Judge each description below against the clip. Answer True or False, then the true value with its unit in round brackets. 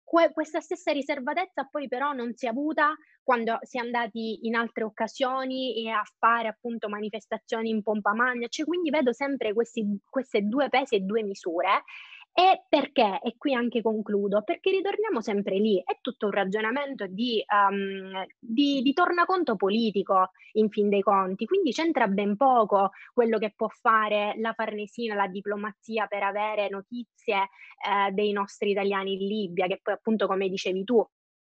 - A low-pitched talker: False (225 Hz)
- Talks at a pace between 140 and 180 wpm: True (165 wpm)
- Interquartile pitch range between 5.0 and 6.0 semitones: False (4.5 semitones)